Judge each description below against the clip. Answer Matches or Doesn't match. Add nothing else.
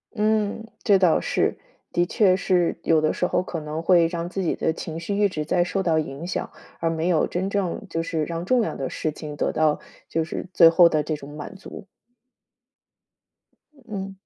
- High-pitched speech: Doesn't match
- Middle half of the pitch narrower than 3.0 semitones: Doesn't match